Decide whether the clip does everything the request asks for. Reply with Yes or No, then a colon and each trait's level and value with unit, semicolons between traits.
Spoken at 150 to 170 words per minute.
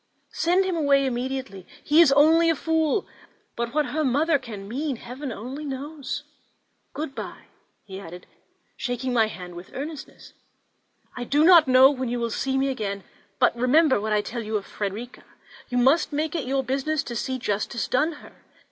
No: average, 180 wpm